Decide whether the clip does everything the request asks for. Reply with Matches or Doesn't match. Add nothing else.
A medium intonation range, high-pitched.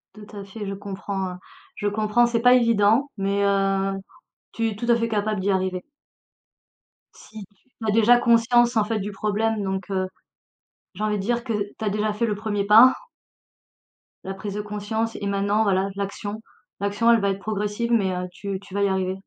Doesn't match